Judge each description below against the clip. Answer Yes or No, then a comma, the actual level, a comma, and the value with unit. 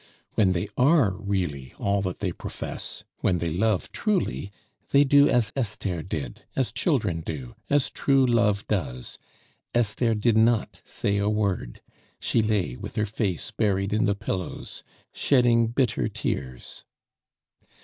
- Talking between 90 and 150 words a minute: Yes, average, 140 wpm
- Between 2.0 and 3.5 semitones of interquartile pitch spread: No, average, 4.4 semitones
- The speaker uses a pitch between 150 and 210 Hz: No, low, 105 Hz